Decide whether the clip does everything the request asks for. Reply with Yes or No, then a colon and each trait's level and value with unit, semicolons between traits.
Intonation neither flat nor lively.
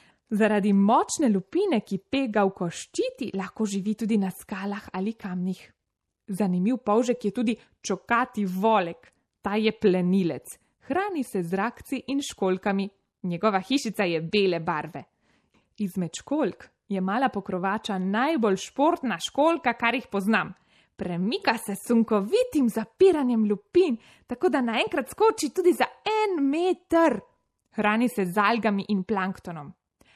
Yes: average, 4.7 semitones